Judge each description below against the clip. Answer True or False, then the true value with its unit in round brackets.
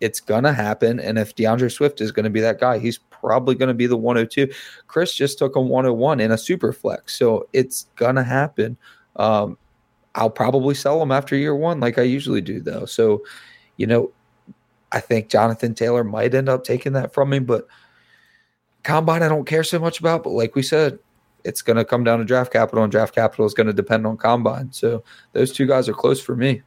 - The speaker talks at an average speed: False (225 wpm)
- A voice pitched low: True (125 Hz)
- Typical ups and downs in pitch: True (3.4 semitones)